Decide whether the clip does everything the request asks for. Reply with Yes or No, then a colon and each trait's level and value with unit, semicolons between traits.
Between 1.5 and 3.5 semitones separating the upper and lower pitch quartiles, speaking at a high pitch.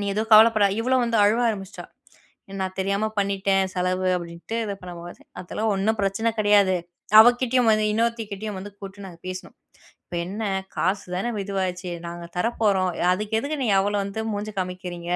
Yes: average, 2.8 semitones; high, 200 Hz